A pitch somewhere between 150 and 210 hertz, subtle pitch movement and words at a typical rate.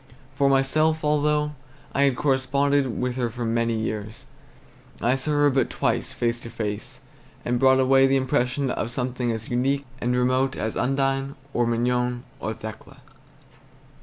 No: low, 130 Hz; narrow, 2.3 semitones; average, 155 wpm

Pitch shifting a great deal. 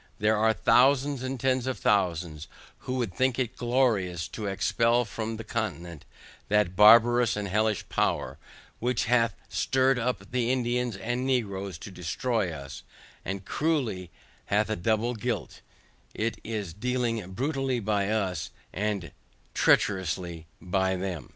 No: average, 4.5 semitones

